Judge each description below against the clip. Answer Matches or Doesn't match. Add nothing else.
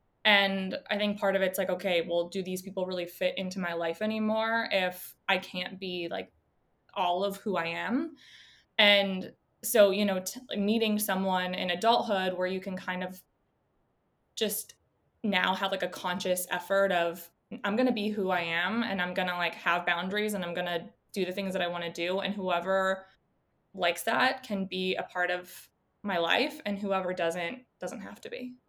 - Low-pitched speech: Doesn't match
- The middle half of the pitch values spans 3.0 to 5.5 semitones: Doesn't match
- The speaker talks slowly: Doesn't match